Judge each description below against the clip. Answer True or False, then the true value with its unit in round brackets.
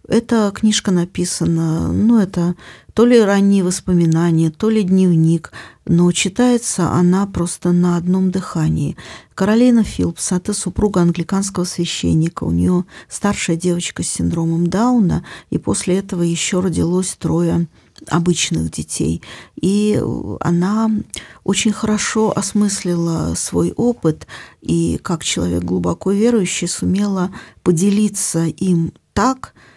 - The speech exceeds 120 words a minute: False (115 wpm)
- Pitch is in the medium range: True (180 Hz)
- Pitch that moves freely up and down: False (3.5 semitones)